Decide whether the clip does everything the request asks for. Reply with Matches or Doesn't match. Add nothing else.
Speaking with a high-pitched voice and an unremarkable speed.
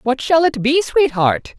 Matches